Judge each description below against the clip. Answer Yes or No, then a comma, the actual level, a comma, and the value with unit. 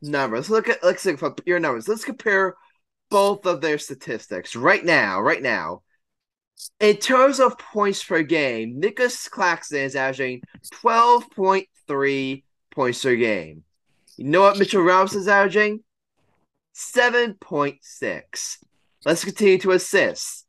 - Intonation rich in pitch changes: Yes, wide, 7.2 semitones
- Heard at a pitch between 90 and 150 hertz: No, high, 190 Hz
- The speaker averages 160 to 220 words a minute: No, average, 145 wpm